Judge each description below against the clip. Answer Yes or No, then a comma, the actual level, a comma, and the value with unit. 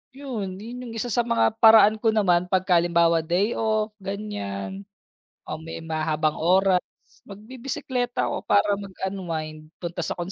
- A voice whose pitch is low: No, high, 195 Hz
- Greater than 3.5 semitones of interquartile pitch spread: Yes, average, 4.4 semitones